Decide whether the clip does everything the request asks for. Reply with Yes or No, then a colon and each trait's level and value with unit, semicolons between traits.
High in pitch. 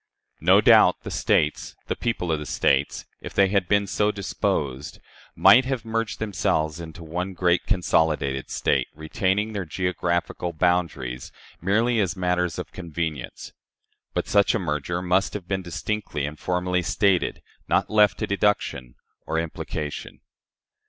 No: very low, 90 Hz